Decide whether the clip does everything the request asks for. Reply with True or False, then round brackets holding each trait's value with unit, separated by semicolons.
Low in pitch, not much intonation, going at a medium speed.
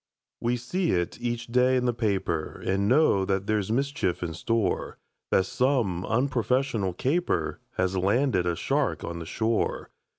False (110 Hz; 5.1 semitones; 155 wpm)